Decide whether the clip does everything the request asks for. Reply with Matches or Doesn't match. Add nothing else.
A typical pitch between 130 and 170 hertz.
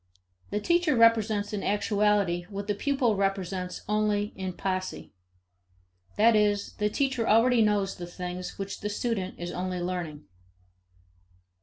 Doesn't match